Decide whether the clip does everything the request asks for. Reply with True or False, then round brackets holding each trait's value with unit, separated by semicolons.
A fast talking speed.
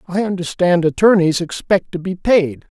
False (150 wpm)